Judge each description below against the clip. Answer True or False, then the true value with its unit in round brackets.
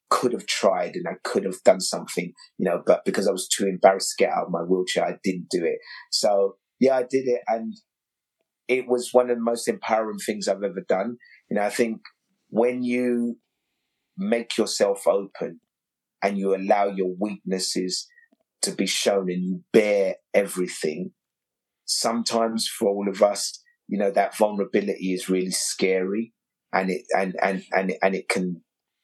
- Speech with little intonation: False (4.5 semitones)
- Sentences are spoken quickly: False (175 wpm)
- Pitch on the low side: True (105 Hz)